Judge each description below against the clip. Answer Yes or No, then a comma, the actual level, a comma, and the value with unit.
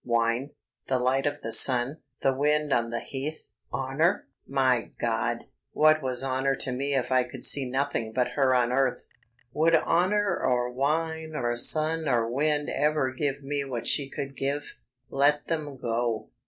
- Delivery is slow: No, average, 165 wpm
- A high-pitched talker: No, low, 135 Hz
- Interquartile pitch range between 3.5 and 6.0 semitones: No, average, 3.0 semitones